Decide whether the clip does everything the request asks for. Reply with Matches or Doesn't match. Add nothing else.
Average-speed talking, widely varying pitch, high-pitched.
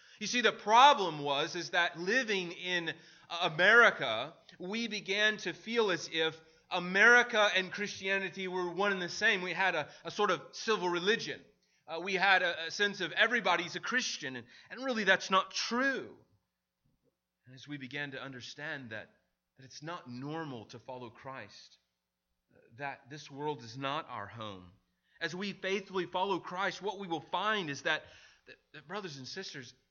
Doesn't match